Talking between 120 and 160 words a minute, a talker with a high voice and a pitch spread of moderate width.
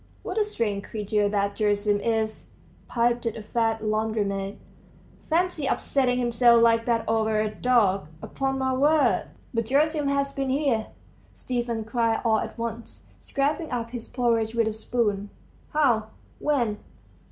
Yes: average, 140 wpm; high, 230 Hz; average, 3.2 semitones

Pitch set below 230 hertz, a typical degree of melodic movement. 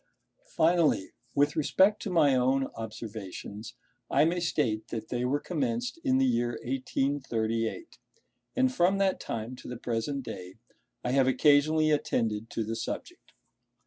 No: low, 135 Hz; wide, 6.7 semitones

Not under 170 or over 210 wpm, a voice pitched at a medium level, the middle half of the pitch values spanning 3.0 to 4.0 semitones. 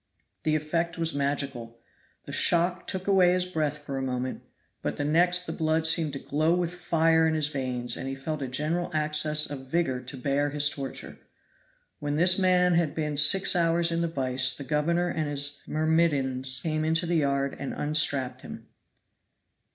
Yes: average, 180 wpm; medium, 155 Hz; average, 3.3 semitones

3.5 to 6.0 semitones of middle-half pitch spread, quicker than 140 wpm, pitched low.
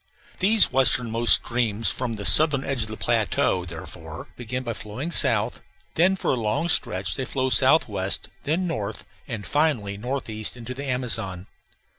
Yes: average, 4.3 semitones; average, 155 wpm; low, 120 Hz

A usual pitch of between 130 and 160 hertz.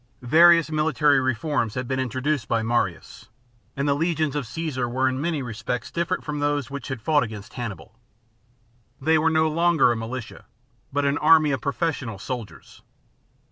Yes: medium, 140 Hz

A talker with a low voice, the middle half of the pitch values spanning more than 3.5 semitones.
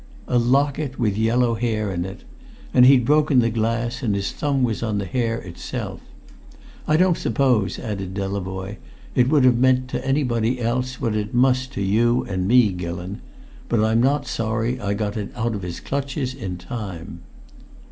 Yes: low, 115 Hz; average, 4.0 semitones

